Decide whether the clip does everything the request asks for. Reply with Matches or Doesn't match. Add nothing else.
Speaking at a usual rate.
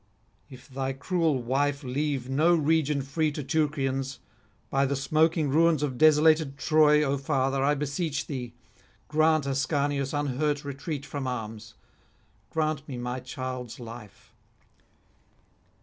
Doesn't match